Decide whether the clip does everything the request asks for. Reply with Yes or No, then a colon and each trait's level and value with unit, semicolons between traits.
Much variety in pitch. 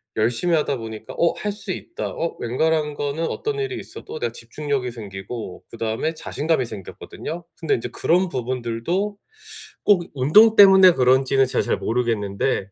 Yes: wide, 7.1 semitones